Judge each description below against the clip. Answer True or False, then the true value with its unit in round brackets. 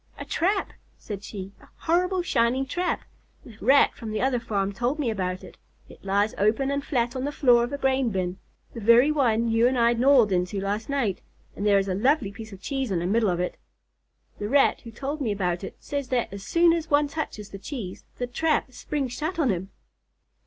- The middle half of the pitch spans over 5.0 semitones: True (5.6 semitones)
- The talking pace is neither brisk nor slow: False (220 wpm)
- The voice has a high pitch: True (235 Hz)